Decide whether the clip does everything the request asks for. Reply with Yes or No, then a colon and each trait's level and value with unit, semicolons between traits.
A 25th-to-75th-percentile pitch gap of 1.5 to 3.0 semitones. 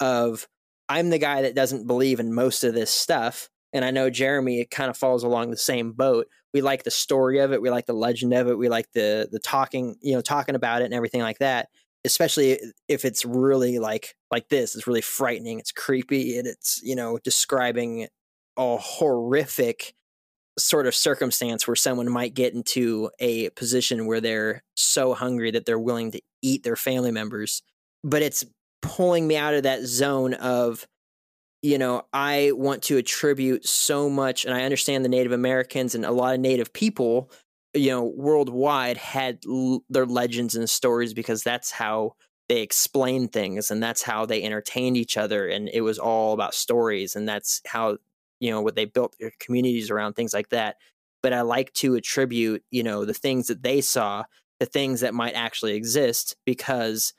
Yes: narrow, 2.4 semitones